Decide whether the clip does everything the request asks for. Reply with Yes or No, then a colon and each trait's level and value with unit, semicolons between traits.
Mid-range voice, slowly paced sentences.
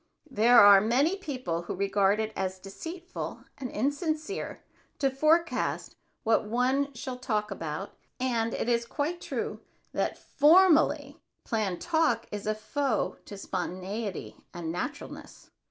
No: high, 235 Hz; slow, 130 wpm